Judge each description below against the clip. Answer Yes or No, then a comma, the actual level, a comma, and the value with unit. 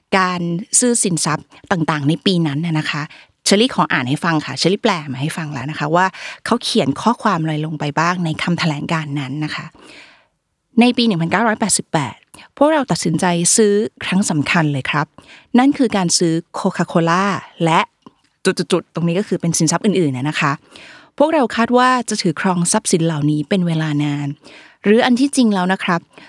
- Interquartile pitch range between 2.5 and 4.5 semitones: No, average, 5.2 semitones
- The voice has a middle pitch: Yes, medium, 175 Hz